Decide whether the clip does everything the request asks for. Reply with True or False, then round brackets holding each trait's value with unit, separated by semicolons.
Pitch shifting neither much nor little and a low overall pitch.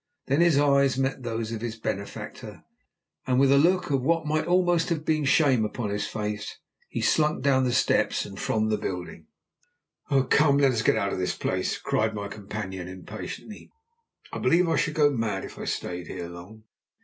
False (6.2 semitones; 125 Hz)